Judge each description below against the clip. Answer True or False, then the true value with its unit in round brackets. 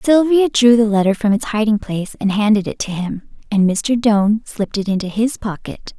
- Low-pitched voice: False (215 Hz)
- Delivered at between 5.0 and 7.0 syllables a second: True (5.4 syllables/s)